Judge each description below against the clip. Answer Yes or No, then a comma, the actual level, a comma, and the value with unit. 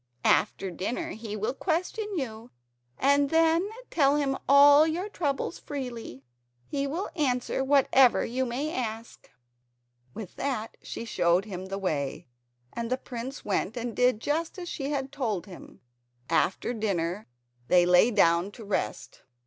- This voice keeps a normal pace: Yes, average, 145 wpm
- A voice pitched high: Yes, very high, 250 Hz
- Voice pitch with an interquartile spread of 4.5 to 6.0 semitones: Yes, wide, 5.4 semitones